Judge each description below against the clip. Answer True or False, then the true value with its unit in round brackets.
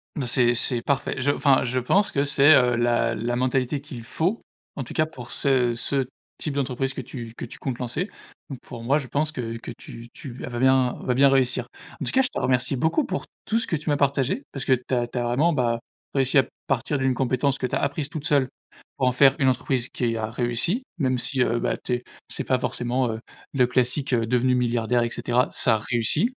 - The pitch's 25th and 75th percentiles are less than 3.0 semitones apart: True (2.6 semitones)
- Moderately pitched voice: False (130 Hz)